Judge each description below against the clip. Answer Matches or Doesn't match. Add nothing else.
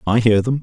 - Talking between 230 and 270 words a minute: Doesn't match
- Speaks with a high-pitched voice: Doesn't match